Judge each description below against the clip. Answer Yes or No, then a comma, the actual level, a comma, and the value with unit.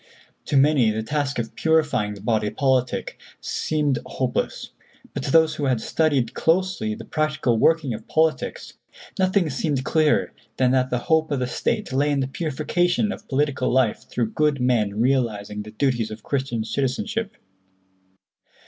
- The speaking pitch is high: No, low, 135 Hz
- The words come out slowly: No, average, 155 wpm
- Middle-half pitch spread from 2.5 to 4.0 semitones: No, average, 4.5 semitones